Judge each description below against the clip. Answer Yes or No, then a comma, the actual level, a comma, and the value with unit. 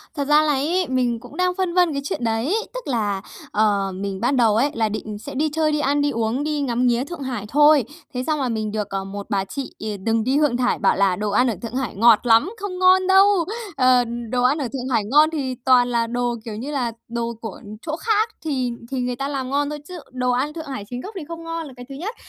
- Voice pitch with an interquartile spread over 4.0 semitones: Yes, average, 4.7 semitones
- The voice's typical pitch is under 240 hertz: No, very high, 255 Hz